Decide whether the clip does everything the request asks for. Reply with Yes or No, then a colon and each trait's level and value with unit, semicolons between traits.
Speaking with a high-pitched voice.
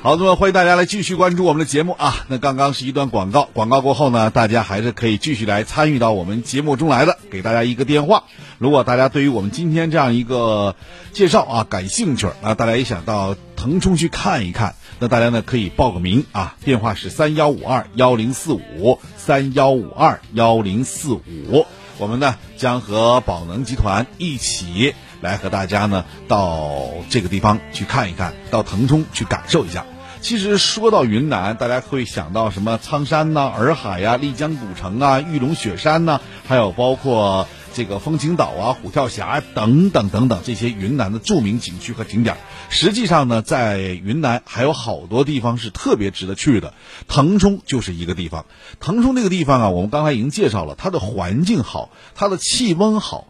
No: low, 120 Hz